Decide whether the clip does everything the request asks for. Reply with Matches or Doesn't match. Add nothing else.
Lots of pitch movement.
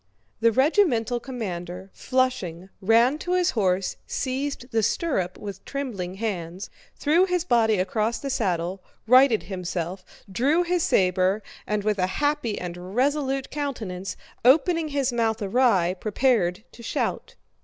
Matches